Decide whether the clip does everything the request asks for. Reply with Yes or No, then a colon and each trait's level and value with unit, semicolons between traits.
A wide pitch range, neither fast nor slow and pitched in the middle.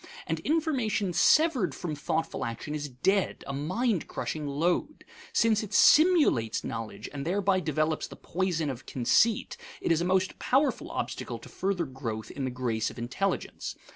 Yes: wide, 7.5 semitones; average, 160 wpm; medium, 165 Hz